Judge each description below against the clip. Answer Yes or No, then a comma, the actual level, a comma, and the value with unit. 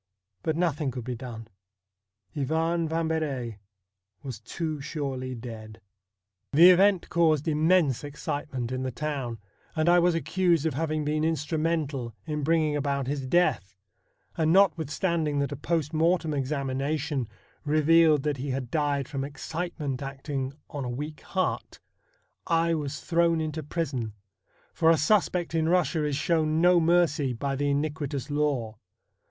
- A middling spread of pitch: Yes, average, 3.2 semitones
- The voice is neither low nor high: Yes, medium, 150 Hz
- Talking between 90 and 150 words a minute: Yes, average, 145 wpm